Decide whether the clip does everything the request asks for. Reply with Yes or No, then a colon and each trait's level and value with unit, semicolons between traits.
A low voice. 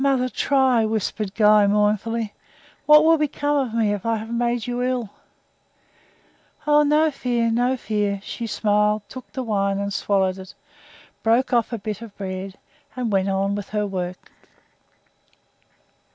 No: high, 220 Hz